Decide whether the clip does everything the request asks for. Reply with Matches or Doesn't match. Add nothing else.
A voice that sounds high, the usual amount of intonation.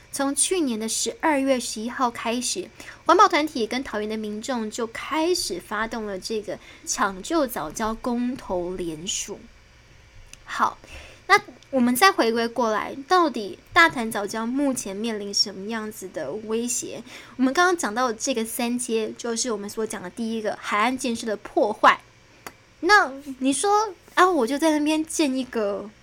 Matches